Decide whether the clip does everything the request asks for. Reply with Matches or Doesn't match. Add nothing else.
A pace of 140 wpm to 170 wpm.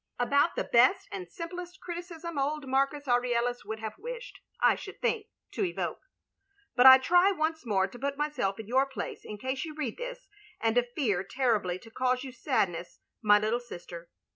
Doesn't match